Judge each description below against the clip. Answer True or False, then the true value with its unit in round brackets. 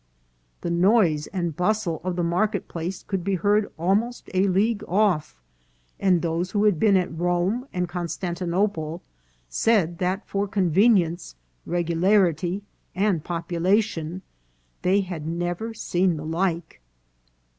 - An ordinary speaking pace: False (130 wpm)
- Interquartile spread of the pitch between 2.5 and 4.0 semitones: True (2.9 semitones)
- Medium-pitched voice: True (180 Hz)